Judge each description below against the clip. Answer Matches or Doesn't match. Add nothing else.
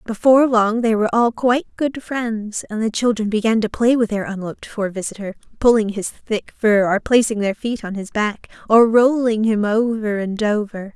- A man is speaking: Doesn't match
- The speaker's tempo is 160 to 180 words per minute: Doesn't match